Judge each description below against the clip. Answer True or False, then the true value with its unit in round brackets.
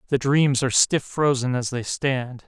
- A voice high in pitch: False (130 Hz)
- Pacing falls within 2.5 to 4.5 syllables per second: True (4.4 syllables/s)